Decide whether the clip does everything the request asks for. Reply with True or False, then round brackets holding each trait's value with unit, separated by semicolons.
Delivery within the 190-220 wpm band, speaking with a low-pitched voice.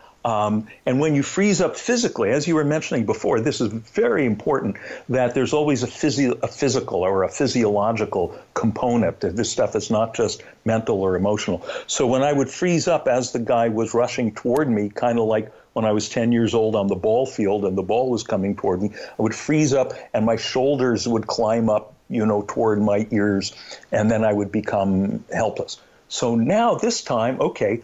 True (205 wpm; 115 Hz)